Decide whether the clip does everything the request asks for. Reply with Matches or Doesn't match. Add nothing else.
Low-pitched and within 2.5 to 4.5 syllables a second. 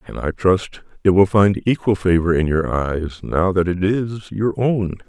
Matches